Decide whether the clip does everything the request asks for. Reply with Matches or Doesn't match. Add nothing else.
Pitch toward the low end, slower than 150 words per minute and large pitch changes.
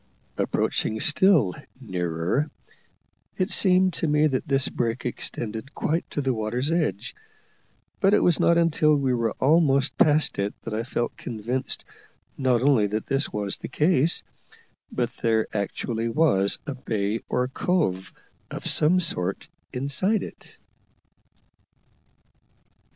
Matches